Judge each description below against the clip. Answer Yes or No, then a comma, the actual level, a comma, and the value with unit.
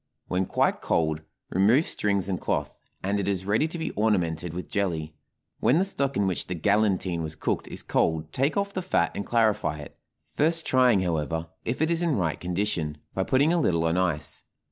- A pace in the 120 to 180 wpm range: No, average, 200 wpm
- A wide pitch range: Yes, wide, 7.6 semitones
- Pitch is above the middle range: No, very low, 95 Hz